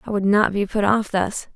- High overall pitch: Yes, high, 205 Hz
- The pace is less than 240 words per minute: No, fast, 270 wpm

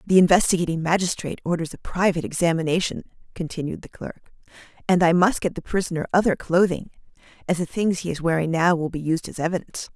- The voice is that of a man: No, female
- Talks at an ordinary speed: Yes, average, 180 wpm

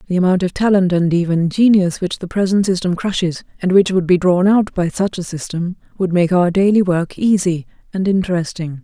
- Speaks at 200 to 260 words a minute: Yes, fast, 205 wpm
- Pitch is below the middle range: No, medium, 180 Hz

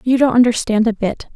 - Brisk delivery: Yes, fast, 220 wpm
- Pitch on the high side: Yes, high, 235 Hz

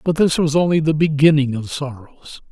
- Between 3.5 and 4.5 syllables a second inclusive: No, 5.1 syllables/s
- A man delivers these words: Yes, male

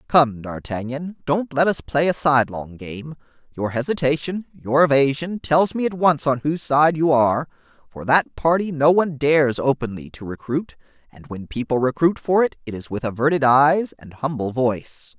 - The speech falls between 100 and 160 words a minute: No, average, 180 wpm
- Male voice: Yes, male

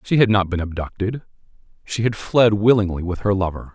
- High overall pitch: No, low, 100 Hz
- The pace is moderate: Yes, average, 175 wpm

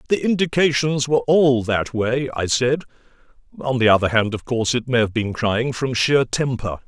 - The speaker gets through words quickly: No, average, 190 wpm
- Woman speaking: No, male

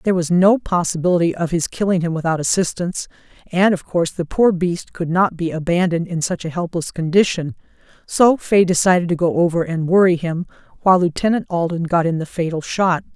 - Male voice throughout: No, female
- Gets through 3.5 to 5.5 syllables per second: No, 5.8 syllables/s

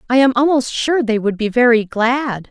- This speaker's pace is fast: Yes, fast, 215 wpm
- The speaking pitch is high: Yes, high, 240 Hz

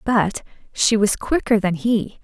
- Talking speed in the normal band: Yes, average, 160 wpm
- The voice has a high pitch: Yes, high, 215 Hz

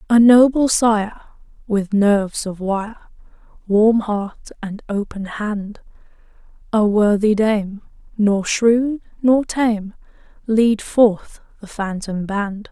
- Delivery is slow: Yes, slow, 115 wpm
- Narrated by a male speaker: No, female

